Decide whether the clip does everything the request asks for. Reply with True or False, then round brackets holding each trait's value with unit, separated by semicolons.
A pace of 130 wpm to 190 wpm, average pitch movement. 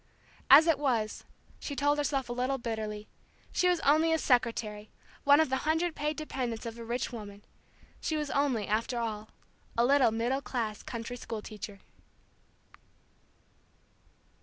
True (150 wpm; 4.5 semitones)